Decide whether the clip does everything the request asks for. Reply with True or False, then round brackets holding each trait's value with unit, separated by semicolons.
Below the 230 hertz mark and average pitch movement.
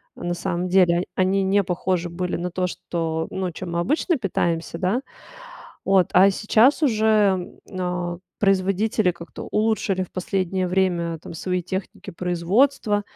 False (185 Hz; 2.1 semitones)